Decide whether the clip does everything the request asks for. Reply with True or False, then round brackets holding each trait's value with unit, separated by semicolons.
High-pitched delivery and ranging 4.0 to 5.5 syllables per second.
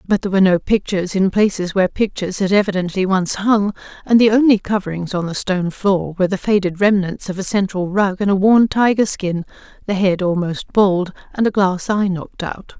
False (195 Hz; 5.7 syllables/s)